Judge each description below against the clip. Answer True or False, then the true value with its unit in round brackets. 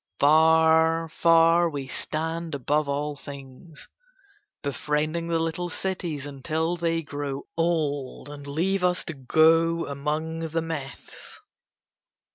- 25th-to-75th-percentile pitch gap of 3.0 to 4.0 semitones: False (2.5 semitones)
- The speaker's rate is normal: False (110 wpm)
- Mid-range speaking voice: True (160 Hz)